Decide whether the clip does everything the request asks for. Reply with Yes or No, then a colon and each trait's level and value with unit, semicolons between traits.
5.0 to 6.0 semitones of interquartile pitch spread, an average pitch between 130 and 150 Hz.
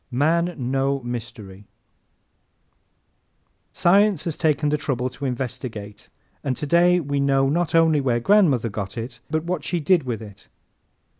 Yes: average, 5.3 semitones; medium, 140 Hz